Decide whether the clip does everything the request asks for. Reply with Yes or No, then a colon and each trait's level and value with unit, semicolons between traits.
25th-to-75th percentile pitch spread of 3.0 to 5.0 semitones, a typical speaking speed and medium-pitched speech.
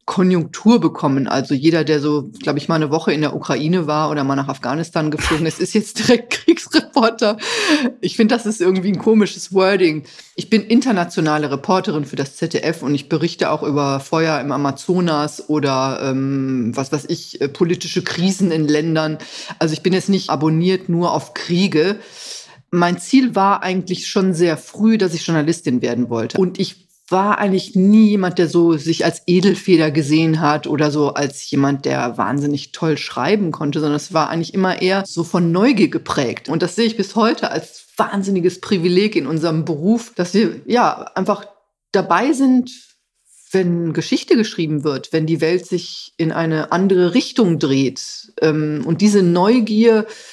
Yes: average, 4.4 semitones; average, 170 wpm; medium, 175 Hz